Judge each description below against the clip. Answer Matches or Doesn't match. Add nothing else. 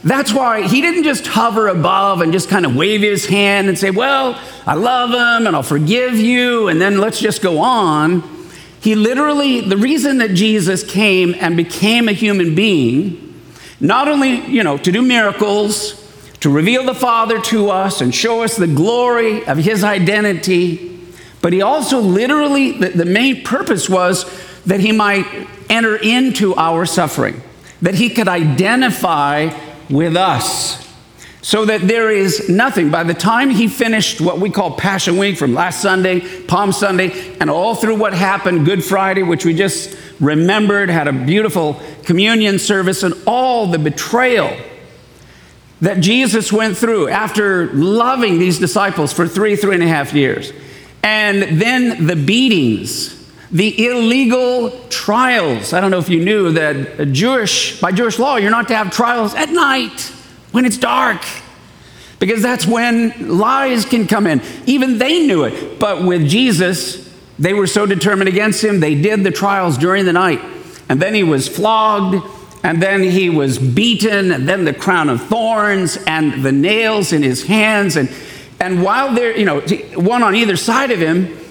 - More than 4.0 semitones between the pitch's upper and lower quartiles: Matches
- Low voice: Doesn't match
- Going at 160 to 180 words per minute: Matches